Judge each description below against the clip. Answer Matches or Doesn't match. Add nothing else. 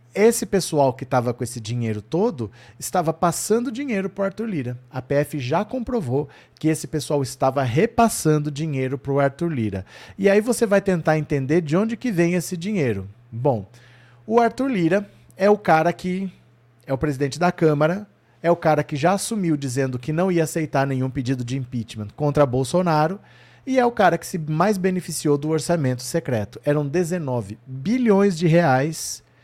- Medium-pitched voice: Matches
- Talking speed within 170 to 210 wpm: Matches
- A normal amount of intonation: Doesn't match